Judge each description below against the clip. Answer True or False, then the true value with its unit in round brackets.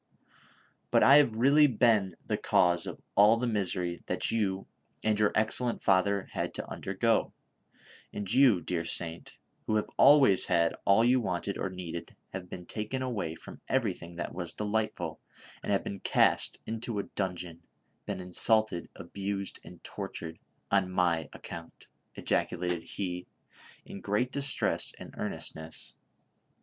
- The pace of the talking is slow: False (150 wpm)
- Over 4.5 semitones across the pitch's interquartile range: False (4.1 semitones)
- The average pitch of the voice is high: False (100 Hz)